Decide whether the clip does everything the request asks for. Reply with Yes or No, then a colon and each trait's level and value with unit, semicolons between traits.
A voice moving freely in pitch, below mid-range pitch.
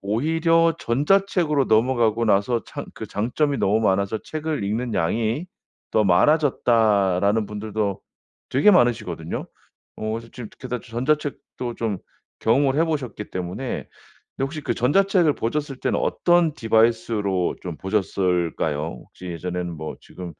Yes: wide, 6.4 semitones; low, 115 Hz